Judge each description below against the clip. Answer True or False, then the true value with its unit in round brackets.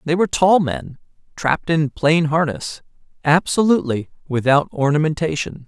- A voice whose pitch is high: False (155 Hz)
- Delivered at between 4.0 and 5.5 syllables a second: True (5.0 syllables/s)